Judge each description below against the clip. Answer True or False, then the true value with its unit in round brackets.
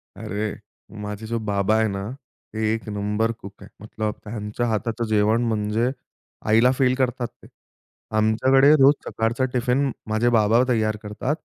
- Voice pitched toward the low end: True (110 Hz)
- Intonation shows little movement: True (2.3 semitones)